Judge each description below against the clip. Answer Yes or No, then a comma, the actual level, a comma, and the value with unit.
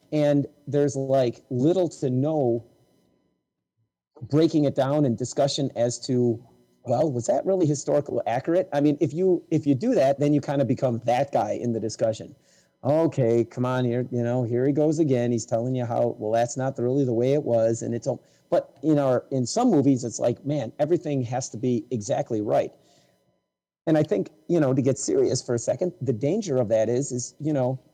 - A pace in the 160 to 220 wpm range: Yes, fast, 205 wpm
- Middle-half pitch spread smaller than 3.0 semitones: No, average, 3.5 semitones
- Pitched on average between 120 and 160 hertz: Yes, low, 135 Hz